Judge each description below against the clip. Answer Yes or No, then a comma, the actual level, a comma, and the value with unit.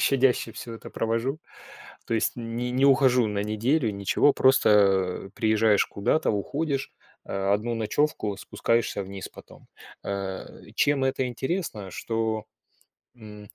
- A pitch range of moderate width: Yes, average, 4.3 semitones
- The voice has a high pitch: No, low, 115 Hz